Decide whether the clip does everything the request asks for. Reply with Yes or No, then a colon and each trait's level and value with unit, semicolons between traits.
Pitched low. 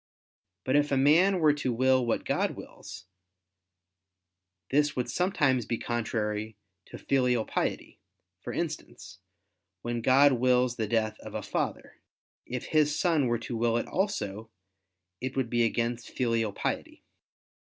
Yes: low, 125 Hz